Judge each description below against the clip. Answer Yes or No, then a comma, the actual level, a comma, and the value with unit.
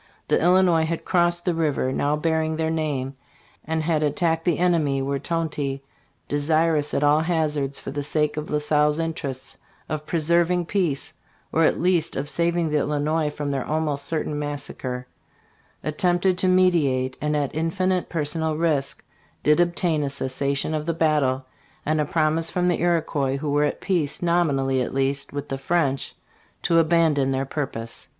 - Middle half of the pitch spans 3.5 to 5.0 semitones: No, average, 2.8 semitones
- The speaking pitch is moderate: Yes, medium, 155 Hz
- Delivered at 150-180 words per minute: Yes, average, 165 wpm